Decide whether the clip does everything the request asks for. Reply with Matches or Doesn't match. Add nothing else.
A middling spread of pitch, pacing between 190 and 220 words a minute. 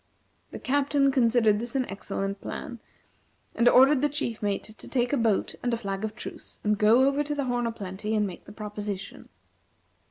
Matches